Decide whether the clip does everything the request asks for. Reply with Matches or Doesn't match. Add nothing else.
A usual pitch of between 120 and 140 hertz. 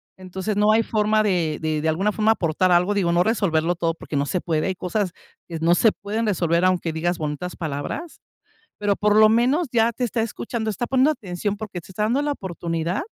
Doesn't match